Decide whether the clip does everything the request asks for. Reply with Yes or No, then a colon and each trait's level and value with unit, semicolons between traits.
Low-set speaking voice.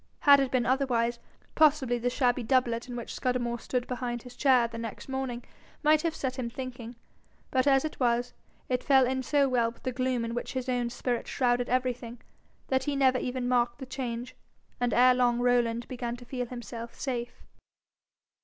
No: very high, 250 Hz